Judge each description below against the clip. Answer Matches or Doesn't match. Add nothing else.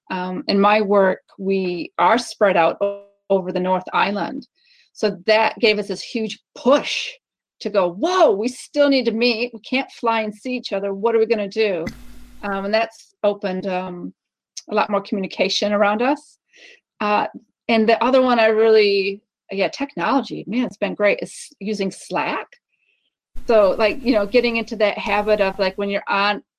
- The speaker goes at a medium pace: Matches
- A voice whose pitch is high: Matches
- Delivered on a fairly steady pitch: Doesn't match